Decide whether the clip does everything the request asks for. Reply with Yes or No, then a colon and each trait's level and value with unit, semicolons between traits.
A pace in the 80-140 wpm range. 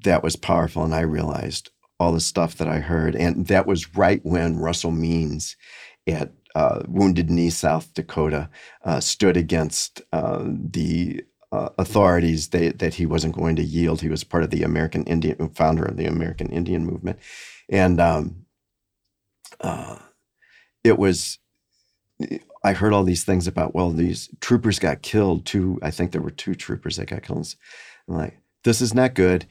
No: average, 170 wpm